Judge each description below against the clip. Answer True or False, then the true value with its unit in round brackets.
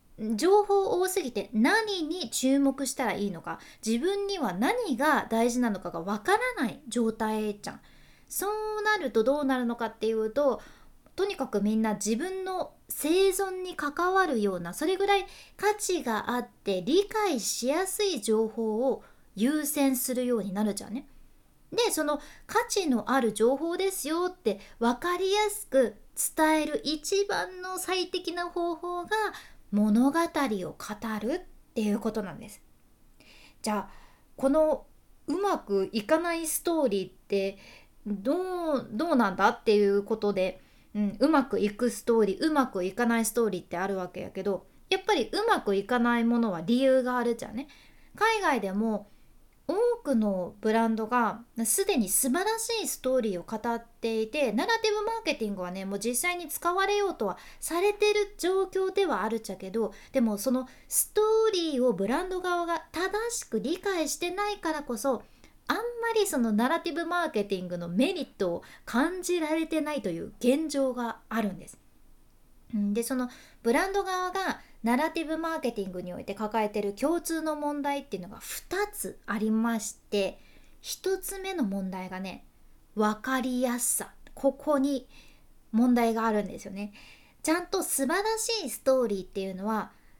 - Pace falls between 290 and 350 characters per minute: True (320 characters per minute)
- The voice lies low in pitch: False (265 Hz)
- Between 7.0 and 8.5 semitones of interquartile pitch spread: True (8.2 semitones)